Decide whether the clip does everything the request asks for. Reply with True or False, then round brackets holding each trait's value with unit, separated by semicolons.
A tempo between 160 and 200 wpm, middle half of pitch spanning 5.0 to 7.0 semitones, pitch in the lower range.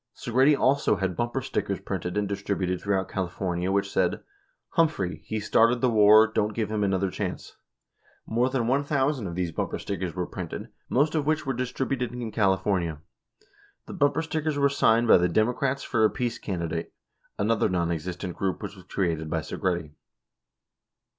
True (170 wpm; 5.5 semitones; 105 Hz)